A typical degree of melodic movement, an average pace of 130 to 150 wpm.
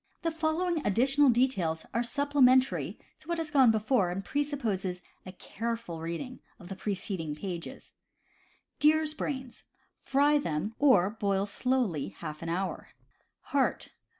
No: wide, 7.3 semitones; average, 145 wpm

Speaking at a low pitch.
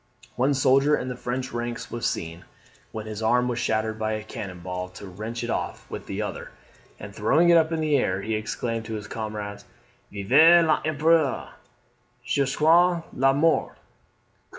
Yes: low, 120 Hz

